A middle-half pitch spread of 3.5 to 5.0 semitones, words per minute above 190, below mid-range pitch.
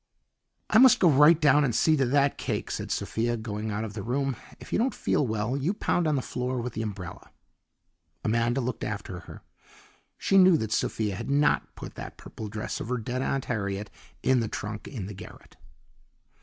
Yes: average, 4.6 semitones; average, 200 wpm; low, 120 Hz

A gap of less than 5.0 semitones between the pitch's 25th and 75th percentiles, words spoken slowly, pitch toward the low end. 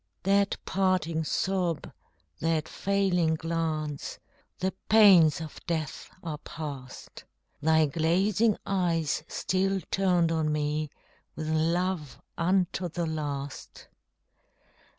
No: average, 3.2 semitones; slow, 95 wpm; medium, 165 Hz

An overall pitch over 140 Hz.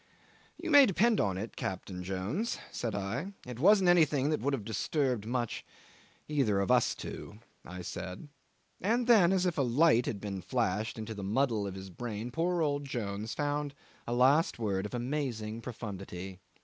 No: low, 120 Hz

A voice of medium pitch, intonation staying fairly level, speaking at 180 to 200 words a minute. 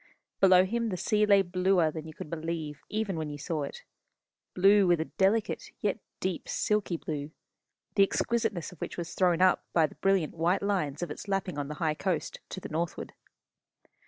No: medium, 180 Hz; average, 3.6 semitones; average, 190 wpm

